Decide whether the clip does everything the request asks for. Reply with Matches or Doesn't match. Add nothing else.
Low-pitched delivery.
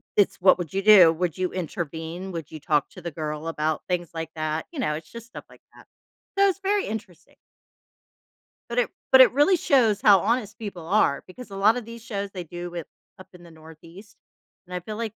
Doesn't match